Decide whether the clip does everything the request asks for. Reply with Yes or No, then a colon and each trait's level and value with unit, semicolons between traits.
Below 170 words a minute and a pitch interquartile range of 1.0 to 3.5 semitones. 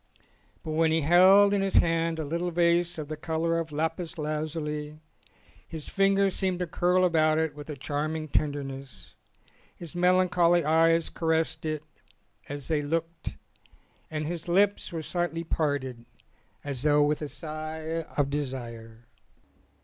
Yes: average, 145 wpm; narrow, 2.4 semitones